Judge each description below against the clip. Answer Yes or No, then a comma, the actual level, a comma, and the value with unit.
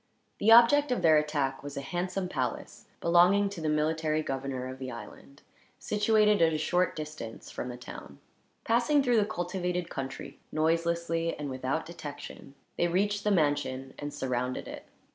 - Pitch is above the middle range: No, medium, 160 Hz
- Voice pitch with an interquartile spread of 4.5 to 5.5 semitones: Yes, average, 5.2 semitones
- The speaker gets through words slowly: No, average, 160 wpm